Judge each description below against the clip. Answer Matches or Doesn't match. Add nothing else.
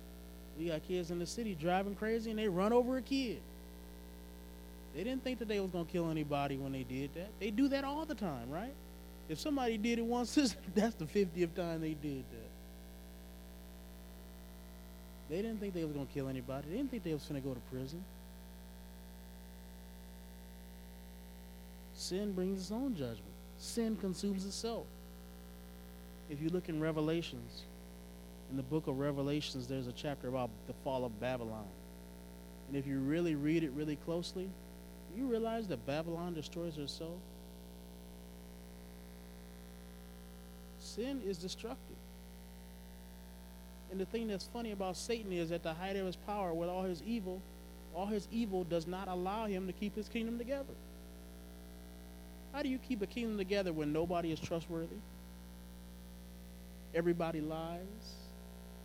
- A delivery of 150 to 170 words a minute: Matches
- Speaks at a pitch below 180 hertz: Matches